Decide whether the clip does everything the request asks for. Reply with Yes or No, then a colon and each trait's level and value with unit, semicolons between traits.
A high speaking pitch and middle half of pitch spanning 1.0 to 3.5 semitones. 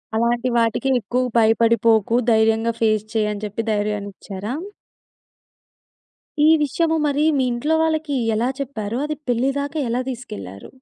No: high, 230 Hz; average, 3.9 semitones